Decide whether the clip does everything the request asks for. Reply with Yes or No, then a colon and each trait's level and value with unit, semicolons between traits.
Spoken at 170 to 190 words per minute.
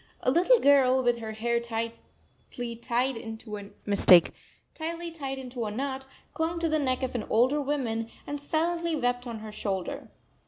No: average, 145 wpm